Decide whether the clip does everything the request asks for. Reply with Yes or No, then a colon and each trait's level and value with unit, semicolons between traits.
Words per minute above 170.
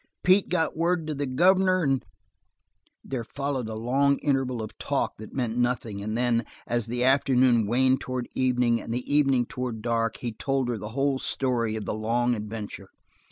Yes: average, 185 wpm